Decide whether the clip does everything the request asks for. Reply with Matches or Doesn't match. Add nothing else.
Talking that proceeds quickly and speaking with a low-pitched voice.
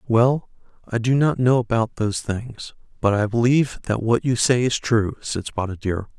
Doesn't match